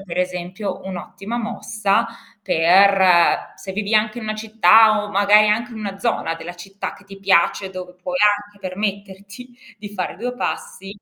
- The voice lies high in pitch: Yes, high, 200 Hz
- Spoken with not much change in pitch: Yes, narrow, 2.3 semitones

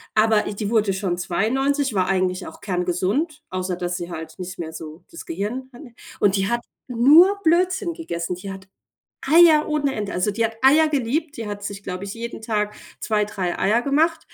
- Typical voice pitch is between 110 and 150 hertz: No, high, 215 Hz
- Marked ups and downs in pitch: Yes, wide, 7.1 semitones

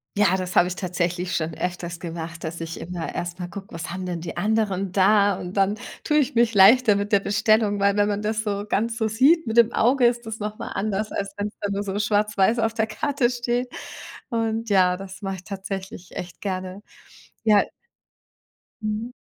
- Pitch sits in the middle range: No, high, 205 Hz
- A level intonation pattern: No, average, 3.1 semitones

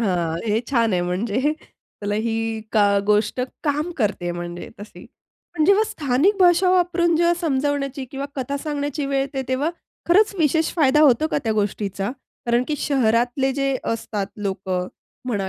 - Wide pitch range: Yes, wide, 6.3 semitones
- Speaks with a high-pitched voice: Yes, very high, 265 Hz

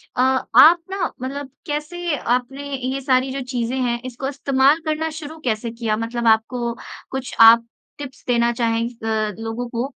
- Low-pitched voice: No, very high, 255 Hz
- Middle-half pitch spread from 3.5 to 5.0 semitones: No, average, 3.1 semitones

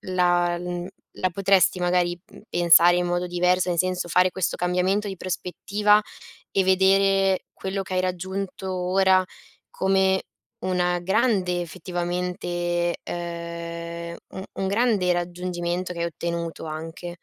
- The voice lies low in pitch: No, medium, 180 Hz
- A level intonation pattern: Yes, narrow, 1.5 semitones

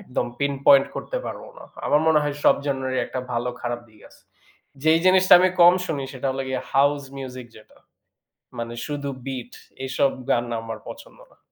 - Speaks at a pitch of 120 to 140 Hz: Yes, low, 135 Hz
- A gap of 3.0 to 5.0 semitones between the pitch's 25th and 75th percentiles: No, narrow, 2.6 semitones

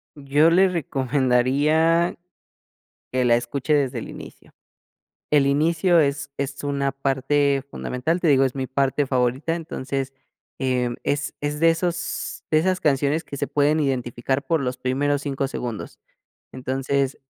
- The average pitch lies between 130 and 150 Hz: Yes, medium, 140 Hz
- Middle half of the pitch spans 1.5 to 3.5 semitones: Yes, narrow, 2.6 semitones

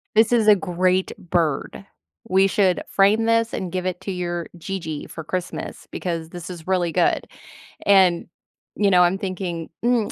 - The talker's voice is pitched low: No, medium, 185 Hz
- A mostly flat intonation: Yes, narrow, 2.2 semitones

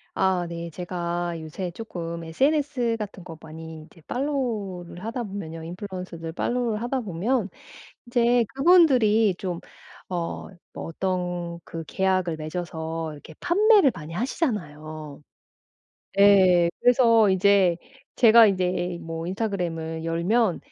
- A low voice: No, medium, 185 Hz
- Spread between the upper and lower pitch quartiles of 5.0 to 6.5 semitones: Yes, average, 5.3 semitones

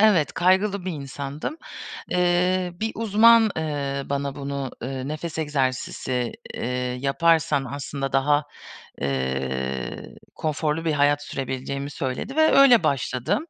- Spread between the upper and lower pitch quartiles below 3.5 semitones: No, average, 4.7 semitones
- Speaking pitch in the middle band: Yes, medium, 145 Hz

